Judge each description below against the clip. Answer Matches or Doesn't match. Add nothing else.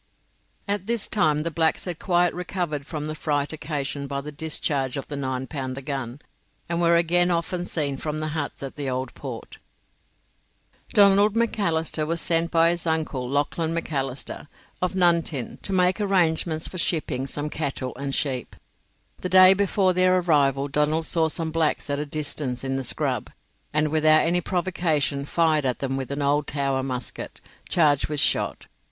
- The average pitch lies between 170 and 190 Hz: Doesn't match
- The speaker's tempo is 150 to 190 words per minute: Matches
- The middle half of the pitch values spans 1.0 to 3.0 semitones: Doesn't match